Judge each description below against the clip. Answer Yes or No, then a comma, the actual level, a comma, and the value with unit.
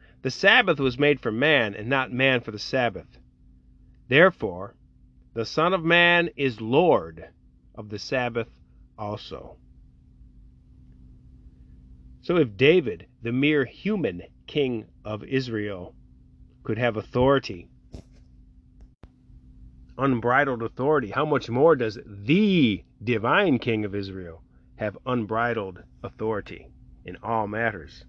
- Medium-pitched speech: No, low, 105 Hz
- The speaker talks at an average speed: No, slow, 110 wpm